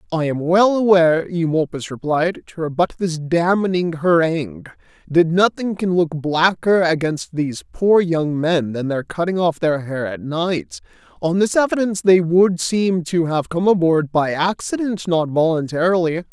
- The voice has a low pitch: No, medium, 170 Hz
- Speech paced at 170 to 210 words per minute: No, average, 160 wpm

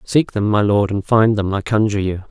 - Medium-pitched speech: No, low, 105 Hz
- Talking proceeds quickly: Yes, fast, 260 wpm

